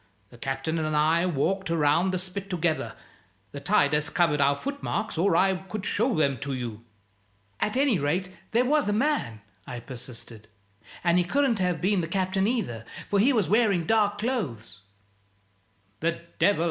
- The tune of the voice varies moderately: No, wide, 6.5 semitones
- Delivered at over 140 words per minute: Yes, average, 170 wpm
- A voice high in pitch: No, medium, 175 Hz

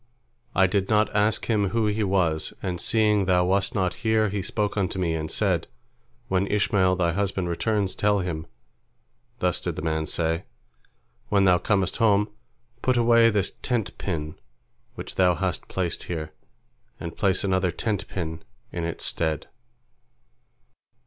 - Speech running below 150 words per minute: No, average, 155 wpm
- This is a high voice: No, very low, 95 Hz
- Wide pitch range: No, average, 3.1 semitones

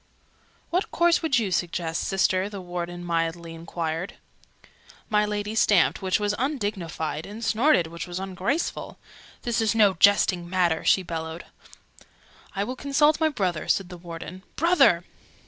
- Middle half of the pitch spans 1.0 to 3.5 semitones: No, average, 4.3 semitones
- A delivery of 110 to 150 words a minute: Yes, average, 145 wpm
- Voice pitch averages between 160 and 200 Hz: Yes, high, 190 Hz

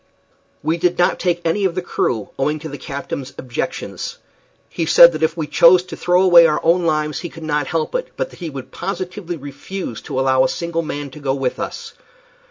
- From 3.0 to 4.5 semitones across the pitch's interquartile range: Yes, average, 3.6 semitones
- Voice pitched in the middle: Yes, medium, 160 Hz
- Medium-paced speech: No, fast, 215 wpm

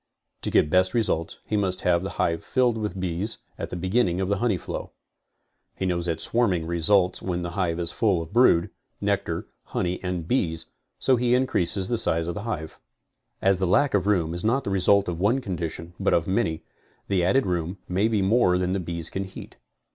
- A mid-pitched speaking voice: No, very low, 95 Hz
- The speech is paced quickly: Yes, fast, 210 wpm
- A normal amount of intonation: Yes, average, 3.4 semitones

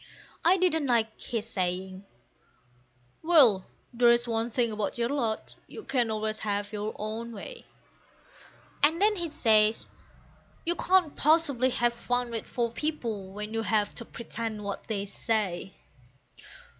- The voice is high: Yes, high, 230 Hz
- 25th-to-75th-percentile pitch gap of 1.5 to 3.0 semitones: No, average, 3.7 semitones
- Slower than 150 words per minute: Yes, average, 140 wpm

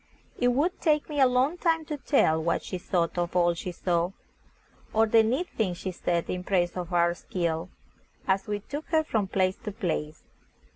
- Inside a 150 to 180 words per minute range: No, average, 195 wpm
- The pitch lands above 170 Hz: Yes, high, 190 Hz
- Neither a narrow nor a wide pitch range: No, wide, 6.6 semitones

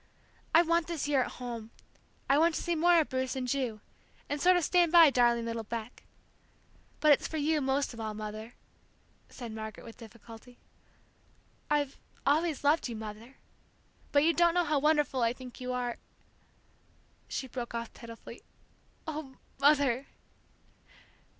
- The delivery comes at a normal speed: Yes, average, 160 wpm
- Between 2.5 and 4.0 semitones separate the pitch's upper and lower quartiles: No, average, 4.8 semitones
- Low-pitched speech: No, very high, 265 Hz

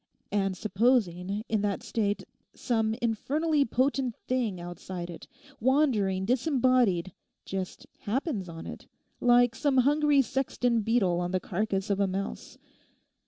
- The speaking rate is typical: No, slow, 120 wpm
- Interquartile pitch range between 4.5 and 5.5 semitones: Yes, average, 5.1 semitones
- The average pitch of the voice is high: Yes, high, 220 Hz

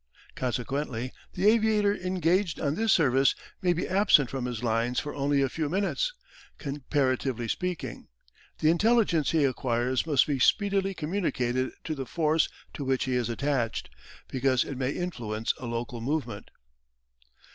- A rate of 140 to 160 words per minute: Yes, average, 145 wpm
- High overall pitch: No, medium, 140 Hz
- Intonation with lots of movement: Yes, wide, 5.9 semitones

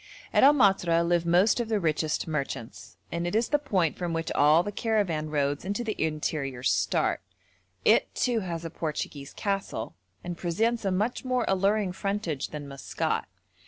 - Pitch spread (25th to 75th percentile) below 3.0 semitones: No, average, 5.1 semitones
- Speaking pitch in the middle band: Yes, medium, 175 Hz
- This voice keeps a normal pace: Yes, average, 170 wpm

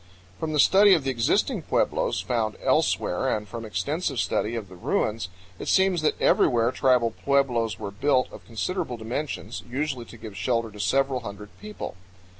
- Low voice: Yes, low, 120 Hz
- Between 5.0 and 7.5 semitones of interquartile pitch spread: No, average, 4.5 semitones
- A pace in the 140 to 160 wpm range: No, average, 170 wpm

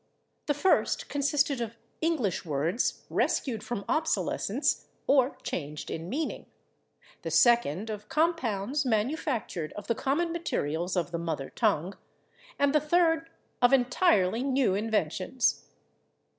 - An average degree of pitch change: No, wide, 7.7 semitones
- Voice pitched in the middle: No, high, 240 Hz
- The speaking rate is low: Yes, slow, 120 wpm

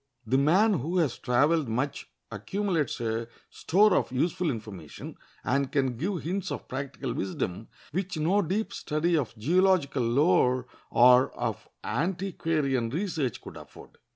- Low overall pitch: No, medium, 145 Hz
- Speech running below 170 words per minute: Yes, slow, 135 wpm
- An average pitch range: No, wide, 6.3 semitones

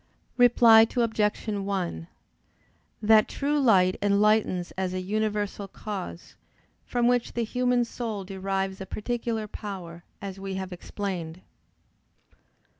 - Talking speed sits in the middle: No, slow, 115 wpm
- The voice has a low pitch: No, high, 205 Hz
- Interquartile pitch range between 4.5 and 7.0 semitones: No, average, 3.0 semitones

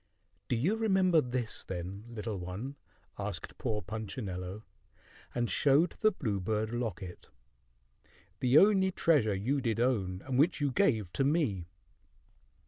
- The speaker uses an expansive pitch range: Yes, wide, 6.4 semitones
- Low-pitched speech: Yes, low, 120 Hz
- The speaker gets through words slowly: Yes, slow, 130 wpm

